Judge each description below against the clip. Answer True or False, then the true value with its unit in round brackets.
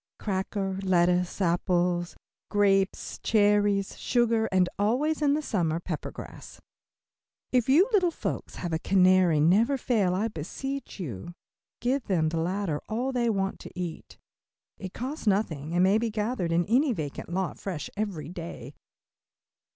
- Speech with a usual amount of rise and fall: True (4.6 semitones)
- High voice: True (195 Hz)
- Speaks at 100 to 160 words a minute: True (150 wpm)